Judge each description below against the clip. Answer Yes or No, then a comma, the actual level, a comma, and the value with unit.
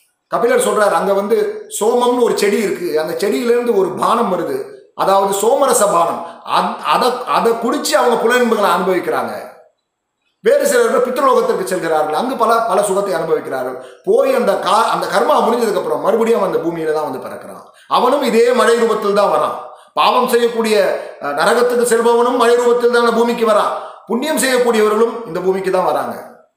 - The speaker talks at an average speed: No, fast, 150 wpm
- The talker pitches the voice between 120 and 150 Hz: No, high, 230 Hz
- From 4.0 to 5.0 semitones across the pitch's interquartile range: Yes, average, 4.3 semitones